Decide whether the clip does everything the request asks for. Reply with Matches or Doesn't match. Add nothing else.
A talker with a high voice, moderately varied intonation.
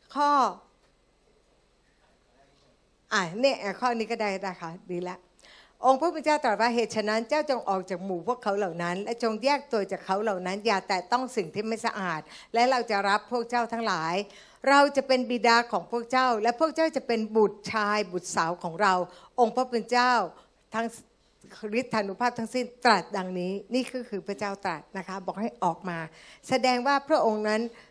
Matches